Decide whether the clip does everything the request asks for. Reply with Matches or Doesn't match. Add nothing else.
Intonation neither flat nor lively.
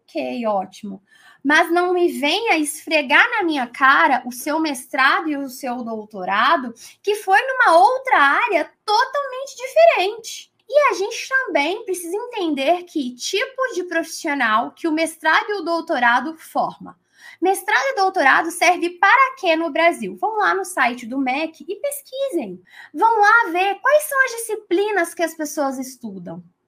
Doesn't match